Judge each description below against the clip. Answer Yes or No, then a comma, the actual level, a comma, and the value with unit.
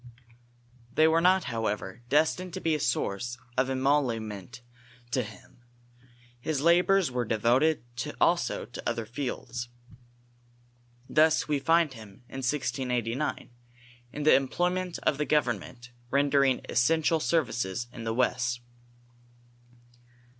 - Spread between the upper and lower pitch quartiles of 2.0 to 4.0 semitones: No, average, 4.7 semitones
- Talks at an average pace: No, slow, 115 wpm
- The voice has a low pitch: Yes, low, 130 Hz